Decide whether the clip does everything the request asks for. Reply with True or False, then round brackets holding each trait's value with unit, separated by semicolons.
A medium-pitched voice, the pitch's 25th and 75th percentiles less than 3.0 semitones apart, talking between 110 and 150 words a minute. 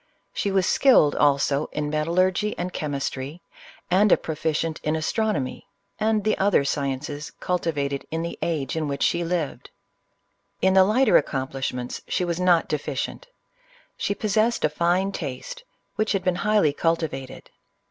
False (165 Hz; 4.7 semitones; 145 wpm)